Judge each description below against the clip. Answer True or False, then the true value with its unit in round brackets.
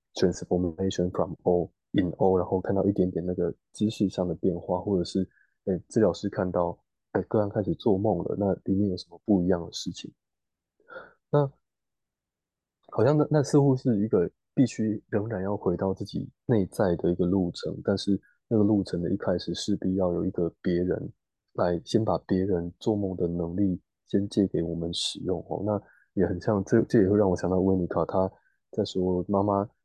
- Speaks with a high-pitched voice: False (95 Hz)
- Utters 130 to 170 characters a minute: False (300 characters per minute)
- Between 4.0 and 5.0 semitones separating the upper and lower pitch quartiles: False (2.8 semitones)